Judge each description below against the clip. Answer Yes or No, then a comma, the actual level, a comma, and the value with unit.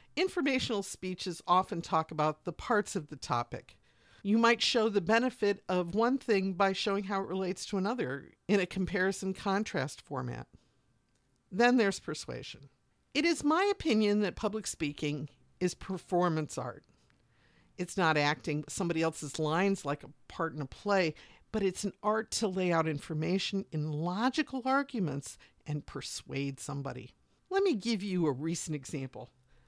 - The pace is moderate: Yes, average, 155 wpm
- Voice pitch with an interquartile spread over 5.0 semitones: Yes, wide, 5.6 semitones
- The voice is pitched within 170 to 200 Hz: Yes, medium, 185 Hz